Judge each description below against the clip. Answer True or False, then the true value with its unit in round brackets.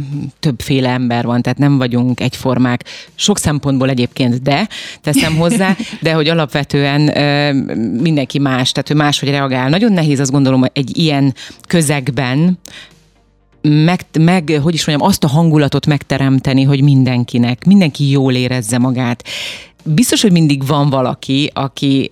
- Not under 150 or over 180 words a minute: False (140 wpm)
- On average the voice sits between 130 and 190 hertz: True (140 Hz)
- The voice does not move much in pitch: False (3.1 semitones)